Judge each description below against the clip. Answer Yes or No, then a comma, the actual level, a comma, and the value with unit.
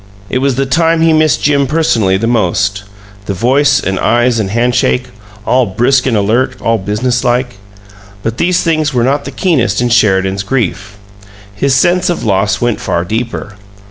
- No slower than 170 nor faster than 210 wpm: Yes, average, 175 wpm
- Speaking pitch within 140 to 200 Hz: No, low, 120 Hz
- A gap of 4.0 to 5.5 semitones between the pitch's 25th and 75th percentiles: Yes, average, 5.0 semitones